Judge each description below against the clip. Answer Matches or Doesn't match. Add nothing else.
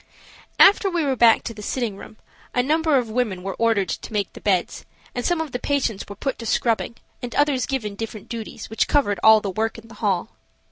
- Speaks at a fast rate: Matches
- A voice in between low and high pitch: Doesn't match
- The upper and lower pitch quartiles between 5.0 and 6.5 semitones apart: Doesn't match